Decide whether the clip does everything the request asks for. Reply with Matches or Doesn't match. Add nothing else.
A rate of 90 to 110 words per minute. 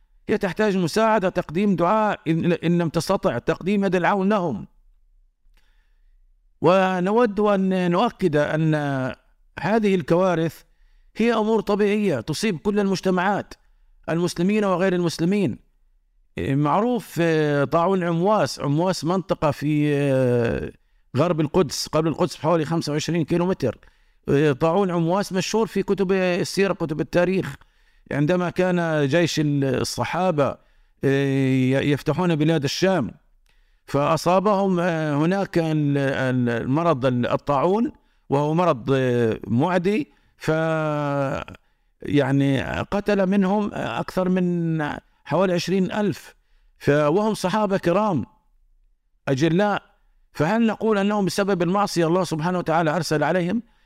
Matches